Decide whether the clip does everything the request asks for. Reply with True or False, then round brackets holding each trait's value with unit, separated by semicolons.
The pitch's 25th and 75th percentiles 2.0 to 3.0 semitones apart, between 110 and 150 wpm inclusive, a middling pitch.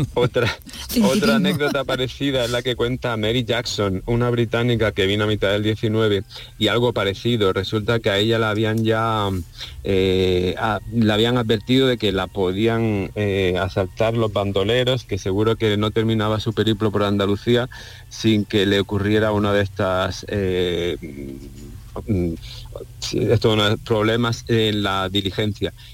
False (2.7 semitones; 140 wpm; 110 Hz)